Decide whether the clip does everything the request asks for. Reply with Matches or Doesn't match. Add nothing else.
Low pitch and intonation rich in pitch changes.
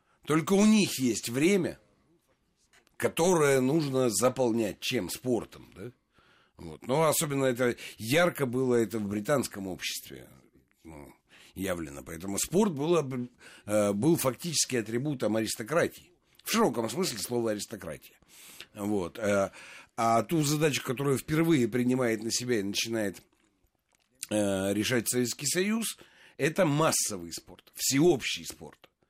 Matches